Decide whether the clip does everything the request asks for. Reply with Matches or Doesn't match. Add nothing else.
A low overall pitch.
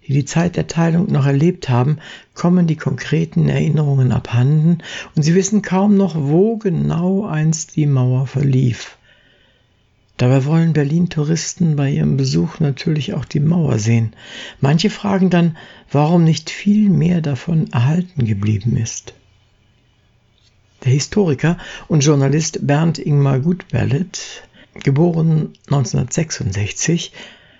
Doesn't match